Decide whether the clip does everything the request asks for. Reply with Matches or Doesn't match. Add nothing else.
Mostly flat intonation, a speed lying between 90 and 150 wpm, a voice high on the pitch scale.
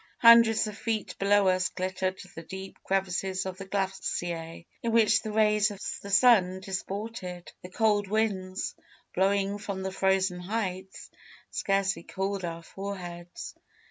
Matches